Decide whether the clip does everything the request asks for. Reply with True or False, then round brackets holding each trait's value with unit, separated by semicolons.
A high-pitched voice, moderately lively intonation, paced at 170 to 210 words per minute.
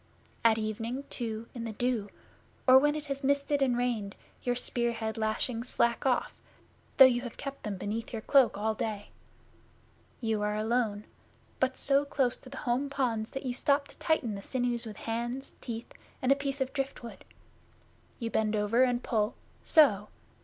True (240 Hz; 3.3 semitones; 175 wpm)